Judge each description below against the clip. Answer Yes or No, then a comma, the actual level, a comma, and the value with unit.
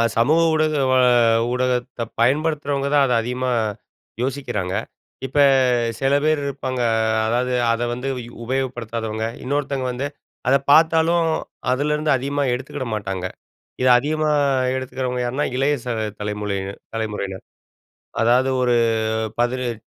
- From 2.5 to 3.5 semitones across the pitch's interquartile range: Yes, average, 3.1 semitones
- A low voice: Yes, low, 130 Hz